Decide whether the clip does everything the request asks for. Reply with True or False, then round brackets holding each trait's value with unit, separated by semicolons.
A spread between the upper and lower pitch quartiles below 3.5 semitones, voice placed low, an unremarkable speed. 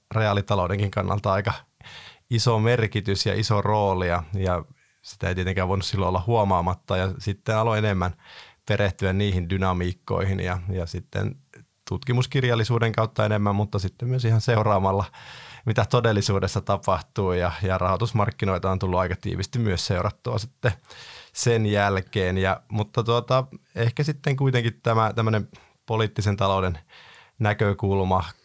True (3.1 semitones; 100 Hz; 125 wpm)